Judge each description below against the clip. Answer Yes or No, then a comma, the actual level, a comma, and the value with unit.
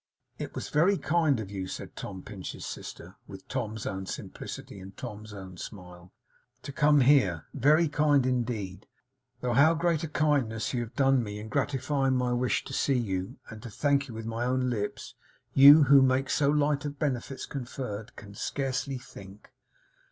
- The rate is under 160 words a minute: No, average, 175 wpm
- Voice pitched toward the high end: No, low, 125 Hz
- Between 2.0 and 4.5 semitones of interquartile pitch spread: No, average, 5.3 semitones